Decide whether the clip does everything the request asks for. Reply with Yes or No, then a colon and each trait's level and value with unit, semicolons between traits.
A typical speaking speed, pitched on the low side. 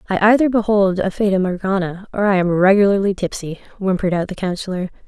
No: average, 175 wpm; high, 190 Hz